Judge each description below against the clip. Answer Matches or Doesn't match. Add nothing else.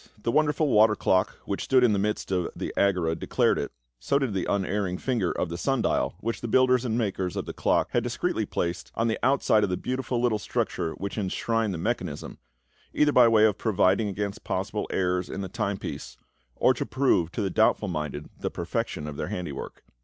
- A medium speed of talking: Doesn't match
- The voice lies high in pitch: Doesn't match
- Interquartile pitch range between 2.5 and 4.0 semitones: Doesn't match